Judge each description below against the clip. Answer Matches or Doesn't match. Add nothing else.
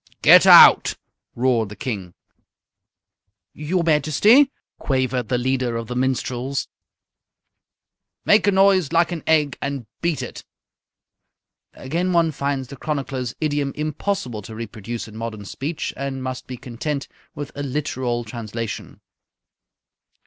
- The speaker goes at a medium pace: Doesn't match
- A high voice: Doesn't match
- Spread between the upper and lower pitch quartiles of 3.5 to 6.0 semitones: Matches